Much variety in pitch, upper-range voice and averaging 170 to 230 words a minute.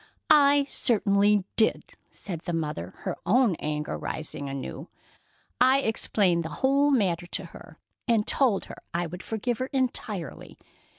No: wide, 7.1 semitones; high, 205 Hz; average, 140 wpm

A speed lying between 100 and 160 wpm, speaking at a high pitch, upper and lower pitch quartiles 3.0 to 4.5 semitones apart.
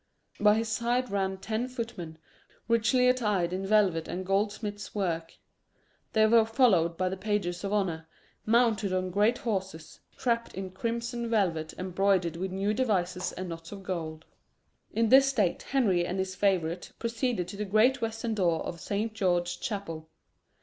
Yes: average, 155 wpm; high, 200 Hz; average, 4.0 semitones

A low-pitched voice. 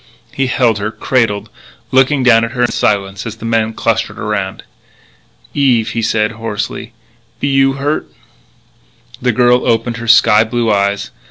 Yes: low, 115 Hz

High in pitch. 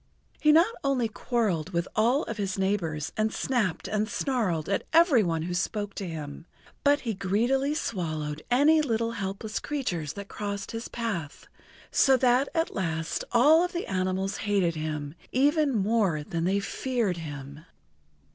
Yes: high, 205 Hz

